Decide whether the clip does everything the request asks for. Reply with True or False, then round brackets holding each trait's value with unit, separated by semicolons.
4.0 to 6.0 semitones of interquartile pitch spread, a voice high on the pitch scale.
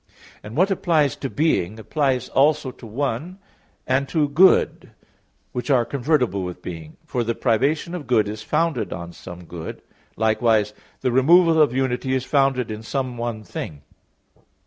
False (5.0 semitones; 125 Hz)